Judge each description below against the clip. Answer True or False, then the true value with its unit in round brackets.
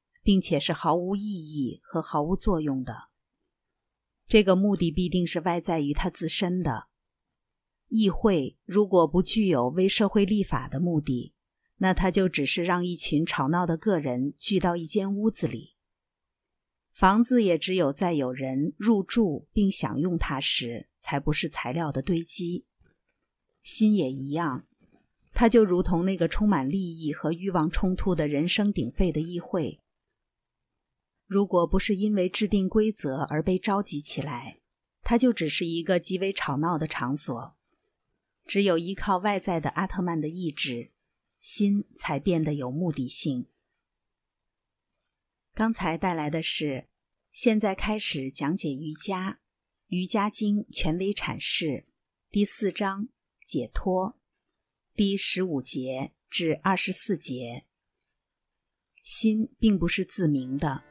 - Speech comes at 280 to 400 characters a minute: False (200 characters per minute)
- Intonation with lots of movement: False (4.6 semitones)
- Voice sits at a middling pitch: True (180 Hz)